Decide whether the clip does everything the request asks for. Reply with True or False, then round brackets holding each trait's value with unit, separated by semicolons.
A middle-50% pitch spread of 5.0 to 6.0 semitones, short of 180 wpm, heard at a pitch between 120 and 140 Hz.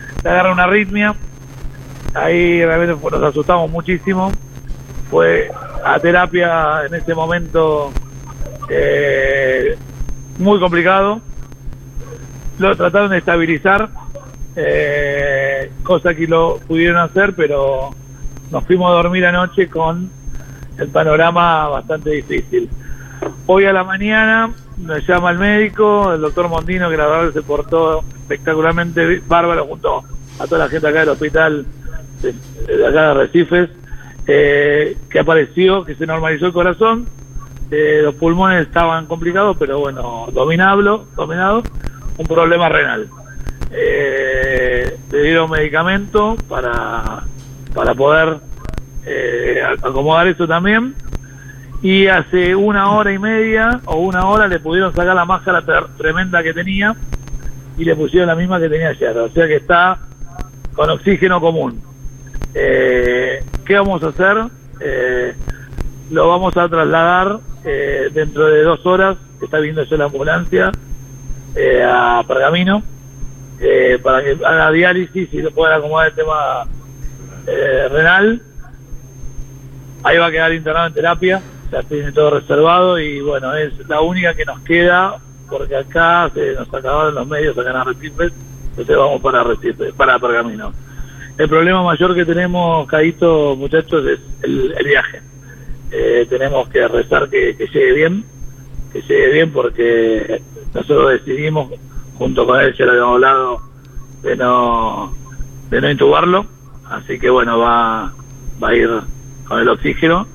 False (5.4 semitones; 140 wpm; 160 Hz)